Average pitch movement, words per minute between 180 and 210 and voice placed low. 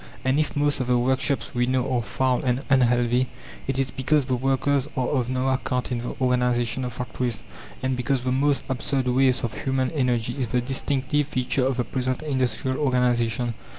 No: narrow, 1.3 semitones; average, 190 wpm; low, 130 Hz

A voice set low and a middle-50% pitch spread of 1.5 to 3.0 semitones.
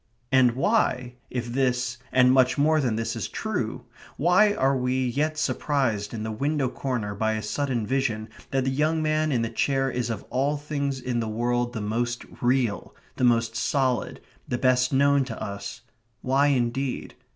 Yes: low, 125 Hz; average, 2.7 semitones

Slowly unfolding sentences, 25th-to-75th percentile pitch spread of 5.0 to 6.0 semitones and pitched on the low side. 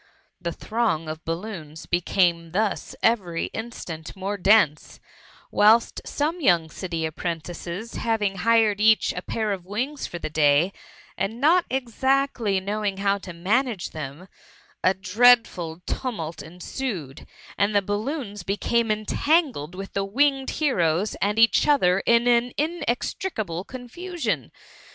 No: slow, 125 wpm; average, 5.3 semitones; high, 205 Hz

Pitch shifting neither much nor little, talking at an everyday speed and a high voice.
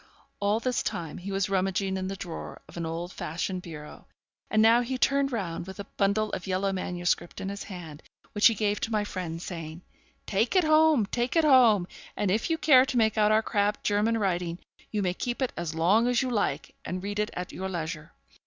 No: average, 4.1 semitones; fast, 220 wpm; high, 200 Hz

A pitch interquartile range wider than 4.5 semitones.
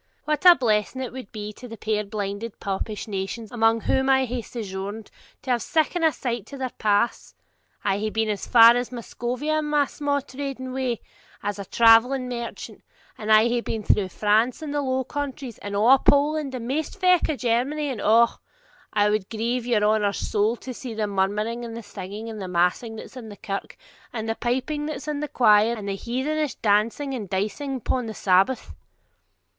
No: average, 3.9 semitones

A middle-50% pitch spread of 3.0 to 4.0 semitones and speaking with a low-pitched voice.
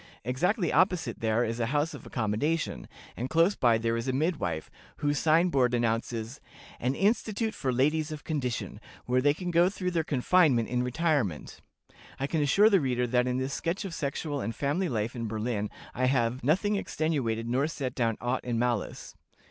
No: wide, 5.4 semitones; low, 130 Hz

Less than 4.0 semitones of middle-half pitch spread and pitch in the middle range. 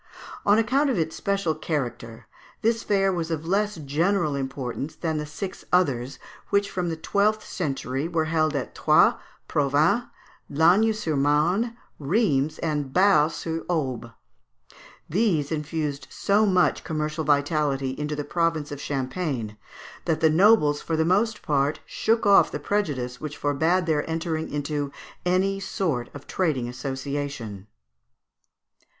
No: average, 4.5 semitones; medium, 155 Hz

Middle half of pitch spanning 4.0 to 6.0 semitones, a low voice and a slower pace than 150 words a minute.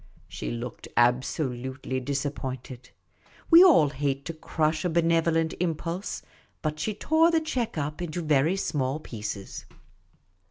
No: average, 4.5 semitones; medium, 155 Hz; slow, 135 wpm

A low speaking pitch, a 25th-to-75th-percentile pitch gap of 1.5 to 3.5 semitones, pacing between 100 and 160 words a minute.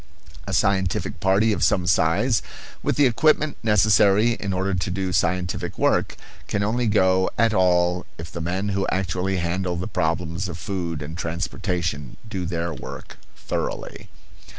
Yes: very low, 95 Hz; narrow, 2.6 semitones; average, 150 wpm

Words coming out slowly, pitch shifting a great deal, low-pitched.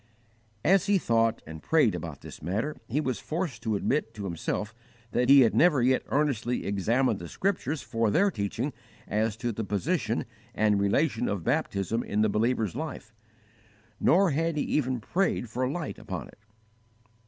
No: average, 165 wpm; wide, 6.1 semitones; low, 120 Hz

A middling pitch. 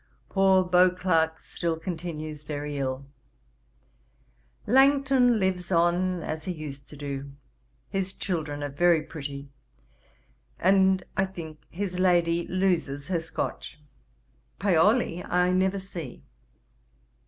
Yes: medium, 175 Hz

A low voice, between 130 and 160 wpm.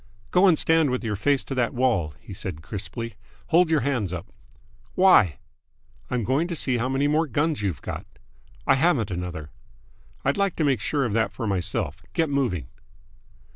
No: low, 125 Hz; average, 180 wpm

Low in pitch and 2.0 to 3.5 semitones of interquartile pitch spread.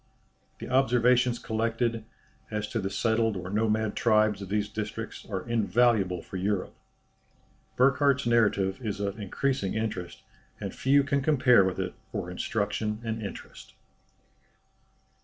Yes: low, 110 Hz; average, 2.9 semitones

